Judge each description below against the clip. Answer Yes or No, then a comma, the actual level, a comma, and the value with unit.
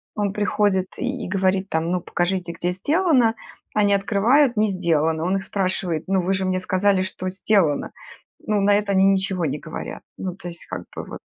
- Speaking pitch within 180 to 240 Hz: Yes, high, 190 Hz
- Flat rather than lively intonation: Yes, narrow, 2.2 semitones